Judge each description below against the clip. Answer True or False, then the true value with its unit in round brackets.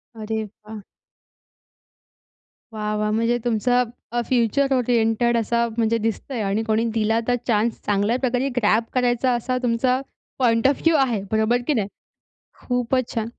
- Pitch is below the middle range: False (230 Hz)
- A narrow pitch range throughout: True (2.1 semitones)